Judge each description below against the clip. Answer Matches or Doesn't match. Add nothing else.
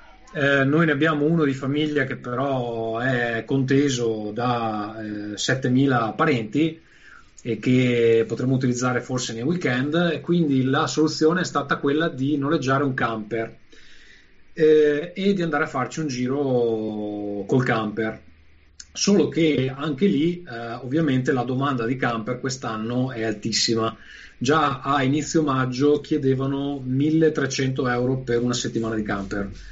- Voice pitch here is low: Matches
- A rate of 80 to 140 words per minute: Matches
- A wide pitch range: Doesn't match